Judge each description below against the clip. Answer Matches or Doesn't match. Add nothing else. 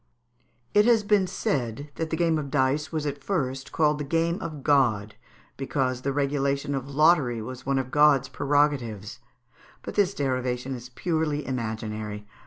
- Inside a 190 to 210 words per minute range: Doesn't match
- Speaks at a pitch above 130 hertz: Matches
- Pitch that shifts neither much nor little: Matches